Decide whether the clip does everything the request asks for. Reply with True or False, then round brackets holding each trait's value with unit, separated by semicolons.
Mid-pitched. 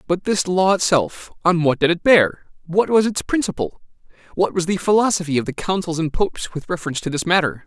True (180 Hz)